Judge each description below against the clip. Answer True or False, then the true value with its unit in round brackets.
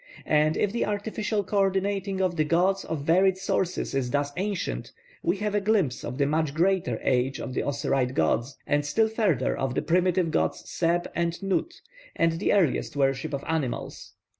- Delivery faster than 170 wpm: True (185 wpm)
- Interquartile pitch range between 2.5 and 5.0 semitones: False (5.4 semitones)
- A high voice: False (170 Hz)